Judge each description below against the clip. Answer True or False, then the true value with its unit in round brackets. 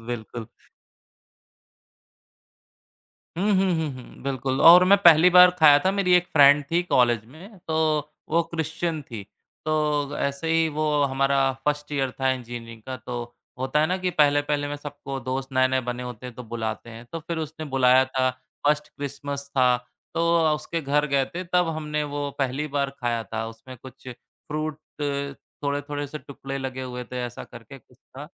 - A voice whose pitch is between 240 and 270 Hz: False (140 Hz)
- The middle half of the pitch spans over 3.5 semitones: False (3.2 semitones)